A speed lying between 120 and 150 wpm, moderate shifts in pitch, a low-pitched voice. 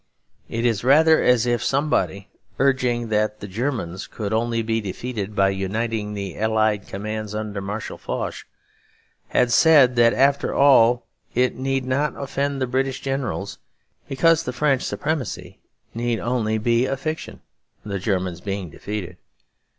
Yes: average, 145 wpm; average, 4.1 semitones; low, 115 Hz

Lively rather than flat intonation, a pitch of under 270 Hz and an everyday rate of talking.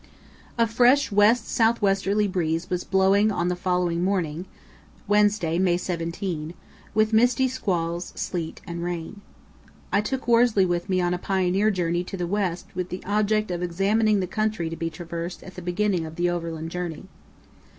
No: average, 3.3 semitones; medium, 185 Hz; average, 170 wpm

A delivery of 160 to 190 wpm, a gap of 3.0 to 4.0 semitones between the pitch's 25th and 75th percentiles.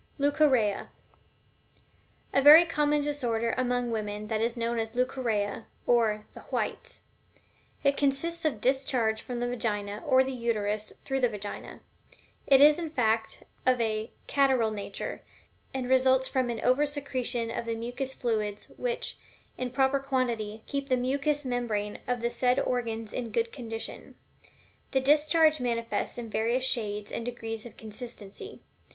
No: average, 150 wpm; average, 3.3 semitones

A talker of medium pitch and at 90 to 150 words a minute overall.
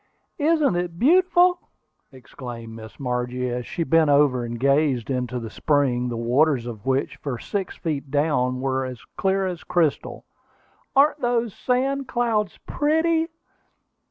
Yes: medium, 145 Hz; average, 140 wpm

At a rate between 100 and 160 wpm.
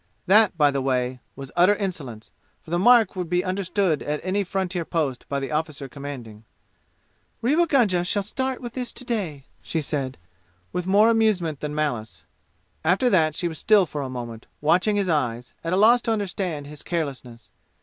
No: average, 180 wpm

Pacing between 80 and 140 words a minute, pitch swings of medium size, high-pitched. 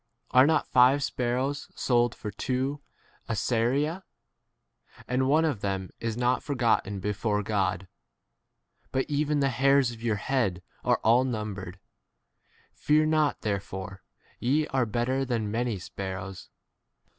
No: slow, 135 wpm; average, 4.7 semitones; low, 120 Hz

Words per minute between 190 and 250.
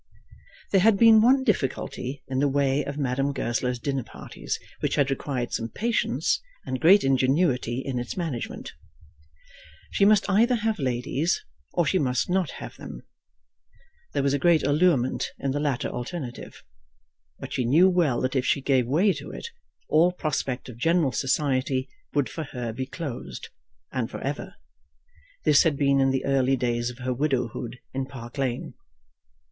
No: average, 165 wpm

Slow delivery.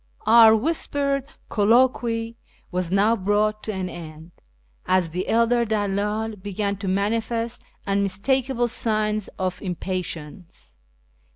Yes: slow, 105 wpm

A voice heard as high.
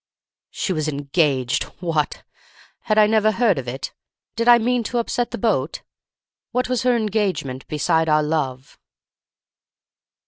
No: medium, 180 Hz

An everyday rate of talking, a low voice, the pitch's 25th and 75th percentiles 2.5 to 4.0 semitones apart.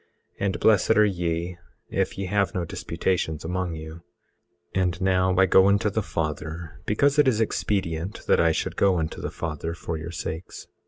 Yes: average, 180 wpm; very low, 90 Hz; average, 3.2 semitones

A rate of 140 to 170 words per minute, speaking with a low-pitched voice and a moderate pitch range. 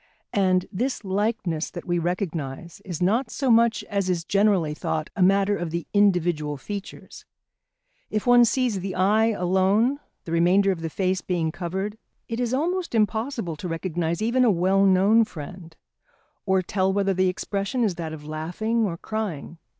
No: average, 165 wpm; high, 190 Hz; average, 4.0 semitones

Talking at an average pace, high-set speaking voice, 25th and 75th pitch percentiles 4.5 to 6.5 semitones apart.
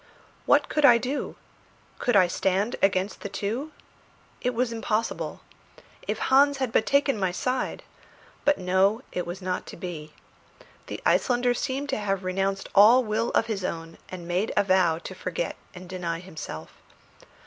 Yes: average, 160 wpm; high, 200 Hz; average, 5.1 semitones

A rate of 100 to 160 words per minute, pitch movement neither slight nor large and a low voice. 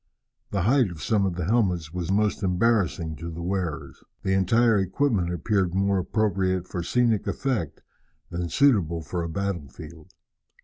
Yes: average, 150 wpm; average, 3.7 semitones; very low, 95 Hz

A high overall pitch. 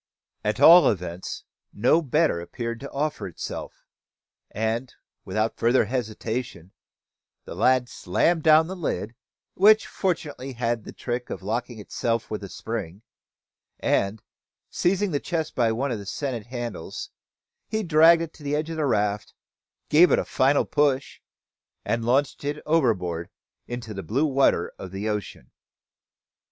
No: low, 120 Hz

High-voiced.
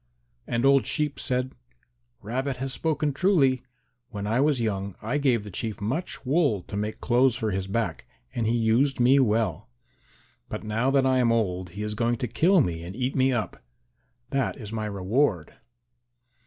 No: low, 120 Hz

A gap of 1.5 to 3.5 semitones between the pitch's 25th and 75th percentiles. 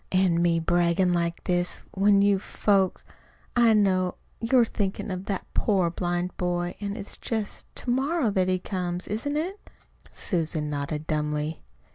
Yes: average, 3.0 semitones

